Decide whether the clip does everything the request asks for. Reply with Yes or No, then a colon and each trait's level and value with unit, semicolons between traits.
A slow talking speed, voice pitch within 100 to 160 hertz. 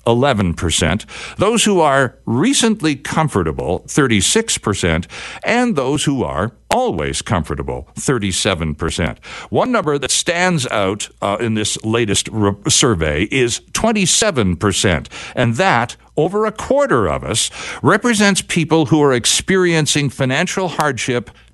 Yes: slow, 115 wpm; medium, 140 Hz